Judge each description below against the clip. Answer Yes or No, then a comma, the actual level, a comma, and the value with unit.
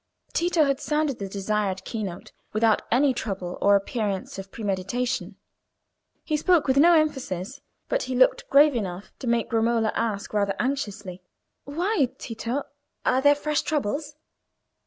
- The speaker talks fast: No, average, 145 wpm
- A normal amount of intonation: No, wide, 6.1 semitones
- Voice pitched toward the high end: Yes, high, 235 Hz